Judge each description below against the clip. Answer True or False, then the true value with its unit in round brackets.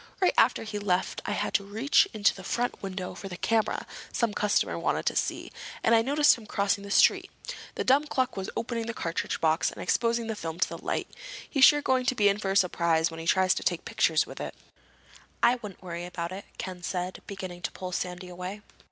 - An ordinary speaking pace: False (225 wpm)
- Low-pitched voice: False (200 Hz)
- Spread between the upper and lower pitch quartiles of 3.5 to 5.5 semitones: True (4.1 semitones)